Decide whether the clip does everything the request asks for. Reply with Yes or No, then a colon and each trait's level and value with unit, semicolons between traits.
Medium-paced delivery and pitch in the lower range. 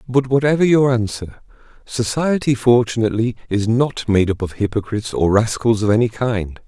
Yes: average, 155 wpm; low, 115 Hz